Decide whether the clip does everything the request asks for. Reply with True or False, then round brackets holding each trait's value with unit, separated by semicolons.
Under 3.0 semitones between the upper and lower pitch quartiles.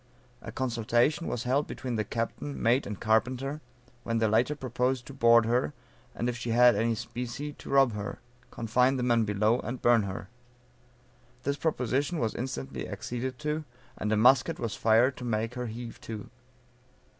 True (2.5 semitones)